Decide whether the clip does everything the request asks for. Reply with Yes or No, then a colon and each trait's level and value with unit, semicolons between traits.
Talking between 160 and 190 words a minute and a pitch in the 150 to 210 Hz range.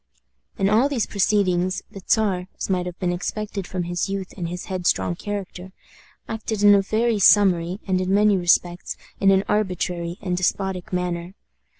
Yes: average, 170 wpm; high, 190 Hz